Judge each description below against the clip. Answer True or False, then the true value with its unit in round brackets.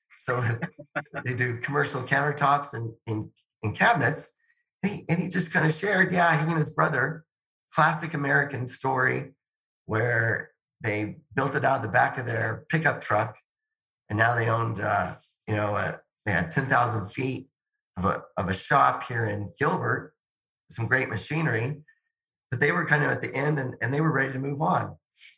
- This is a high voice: False (135 Hz)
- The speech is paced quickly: False (180 wpm)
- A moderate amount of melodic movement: False (5.8 semitones)